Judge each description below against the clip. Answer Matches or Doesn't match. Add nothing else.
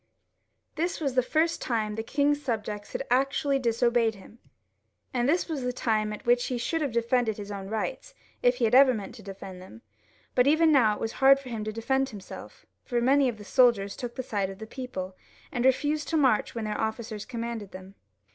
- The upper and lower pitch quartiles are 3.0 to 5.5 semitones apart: Matches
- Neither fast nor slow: Doesn't match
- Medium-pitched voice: Doesn't match